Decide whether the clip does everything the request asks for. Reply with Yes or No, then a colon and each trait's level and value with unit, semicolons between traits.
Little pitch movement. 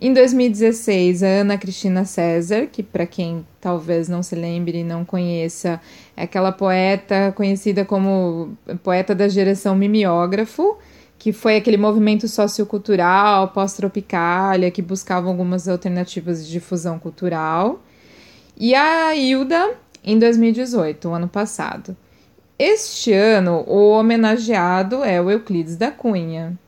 No: average, 3.4 semitones